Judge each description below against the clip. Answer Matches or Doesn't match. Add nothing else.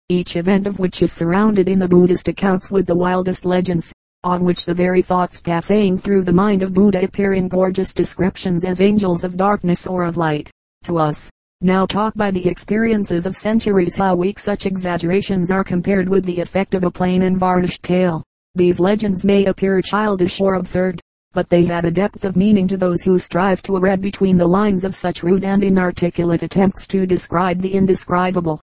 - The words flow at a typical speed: Matches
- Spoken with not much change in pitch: Matches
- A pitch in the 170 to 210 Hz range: Matches